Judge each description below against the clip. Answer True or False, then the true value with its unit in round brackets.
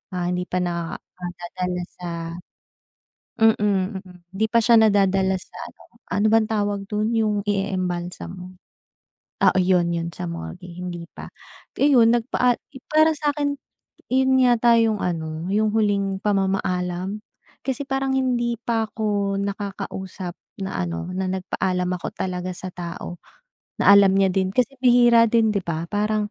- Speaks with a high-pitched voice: True (195 Hz)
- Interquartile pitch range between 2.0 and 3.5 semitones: False (4.0 semitones)